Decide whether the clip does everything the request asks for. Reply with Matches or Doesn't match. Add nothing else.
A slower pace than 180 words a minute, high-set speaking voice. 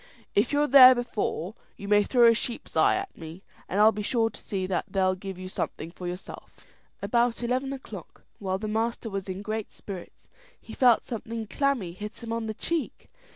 Doesn't match